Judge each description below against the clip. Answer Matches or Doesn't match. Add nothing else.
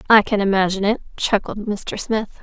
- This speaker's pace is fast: Doesn't match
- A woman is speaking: Matches